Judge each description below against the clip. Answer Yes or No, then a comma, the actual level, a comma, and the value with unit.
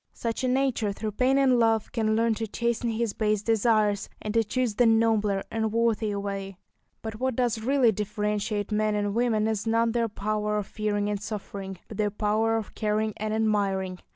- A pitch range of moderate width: No, narrow, 1.7 semitones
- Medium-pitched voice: No, high, 215 Hz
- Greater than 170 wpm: Yes, average, 190 wpm